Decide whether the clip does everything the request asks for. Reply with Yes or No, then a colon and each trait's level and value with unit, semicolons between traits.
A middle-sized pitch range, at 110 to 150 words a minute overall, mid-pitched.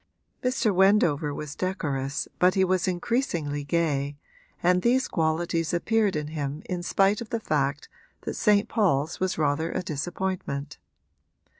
Yes: average, 4.6 semitones; average, 140 wpm; medium, 170 Hz